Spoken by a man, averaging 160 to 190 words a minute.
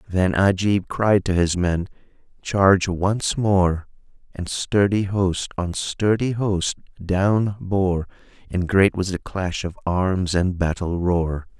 No: male; average, 140 wpm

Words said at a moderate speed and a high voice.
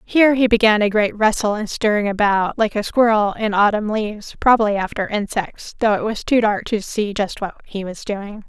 No: fast, 210 wpm; high, 210 Hz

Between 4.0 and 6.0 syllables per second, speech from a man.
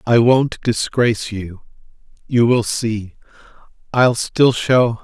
No: 3.4 syllables/s; male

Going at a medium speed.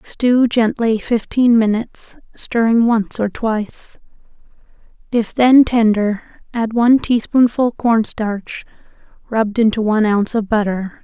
No: slow, 115 wpm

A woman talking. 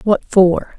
Yes: female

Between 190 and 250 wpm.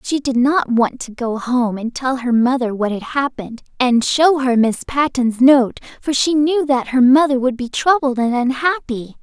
Yes: average, 200 wpm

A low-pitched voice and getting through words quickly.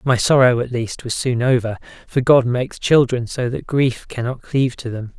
Yes: low, 125 Hz; fast, 210 wpm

